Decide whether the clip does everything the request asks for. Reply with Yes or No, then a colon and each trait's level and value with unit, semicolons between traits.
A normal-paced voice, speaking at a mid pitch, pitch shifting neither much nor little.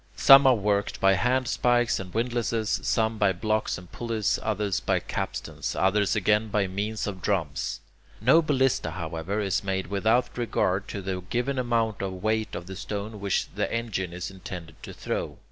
No: average, 170 wpm; low, 105 Hz; average, 3.3 semitones